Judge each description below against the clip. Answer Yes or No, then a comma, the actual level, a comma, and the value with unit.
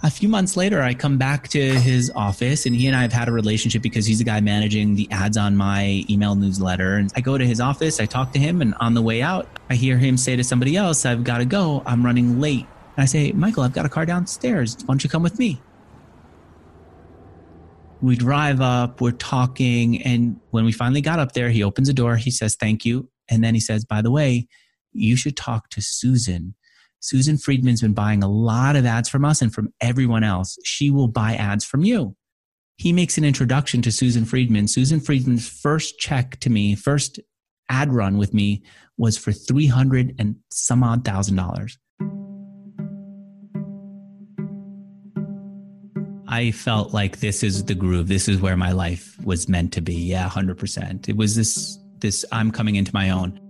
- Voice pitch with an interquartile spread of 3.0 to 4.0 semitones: No, average, 5.3 semitones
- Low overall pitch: Yes, low, 120 Hz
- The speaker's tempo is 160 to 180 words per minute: No, average, 200 wpm